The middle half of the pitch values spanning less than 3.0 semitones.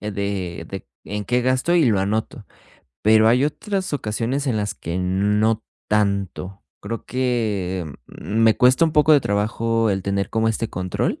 No: average, 3.9 semitones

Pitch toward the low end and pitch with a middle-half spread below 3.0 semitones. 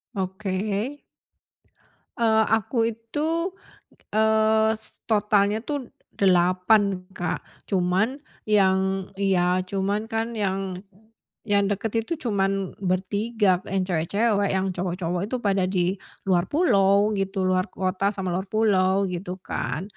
No: high, 195 Hz; narrow, 2.6 semitones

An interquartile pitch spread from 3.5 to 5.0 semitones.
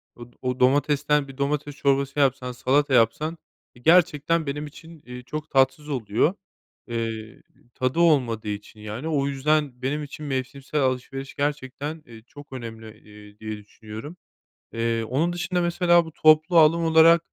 Yes: average, 3.9 semitones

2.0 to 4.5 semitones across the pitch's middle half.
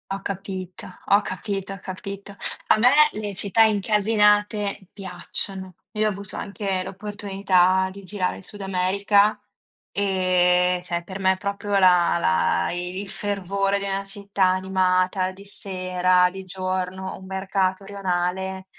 No: narrow, 1.5 semitones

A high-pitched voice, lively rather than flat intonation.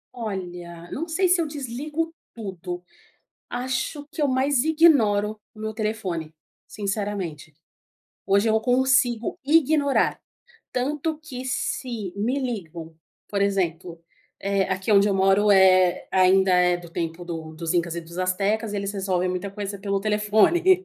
Yes: high, 205 Hz; wide, 5.7 semitones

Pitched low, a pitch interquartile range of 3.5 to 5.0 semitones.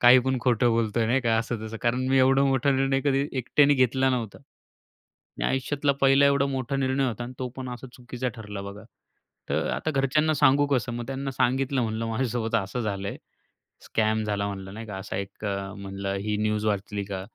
Yes: low, 120 Hz; average, 4.0 semitones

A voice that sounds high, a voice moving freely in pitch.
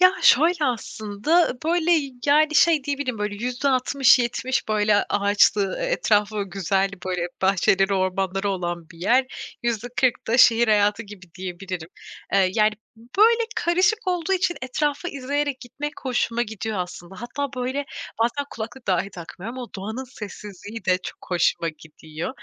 Yes: high, 225 Hz; wide, 6.3 semitones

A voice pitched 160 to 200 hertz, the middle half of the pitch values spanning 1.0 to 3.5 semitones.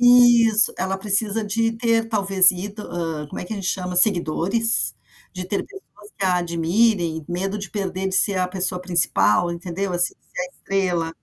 Yes: high, 190 Hz; average, 3.1 semitones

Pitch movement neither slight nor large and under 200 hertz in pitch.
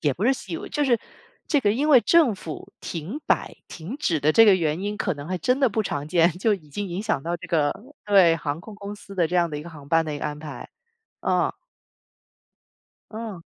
No: wide, 5.8 semitones; medium, 185 Hz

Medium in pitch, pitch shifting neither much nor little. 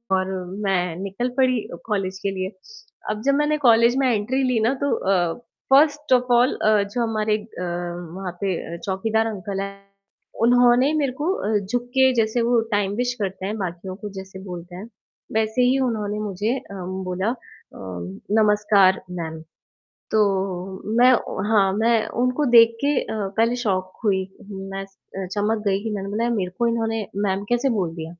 No: high, 215 Hz; average, 3.8 semitones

